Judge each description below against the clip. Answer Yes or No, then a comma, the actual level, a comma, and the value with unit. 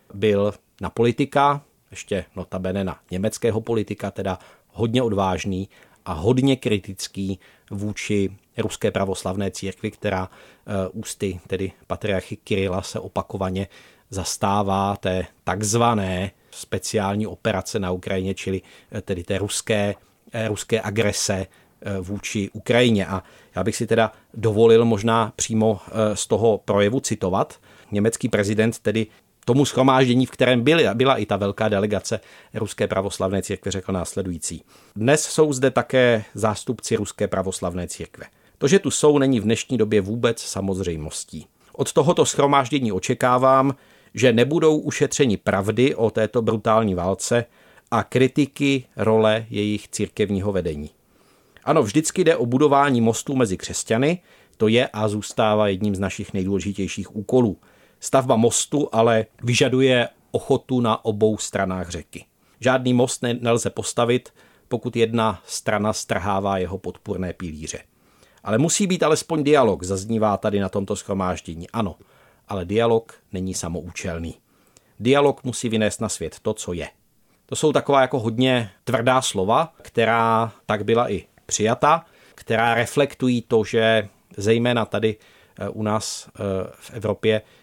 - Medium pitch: No, low, 110 Hz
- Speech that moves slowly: No, average, 130 wpm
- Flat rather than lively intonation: No, average, 3.7 semitones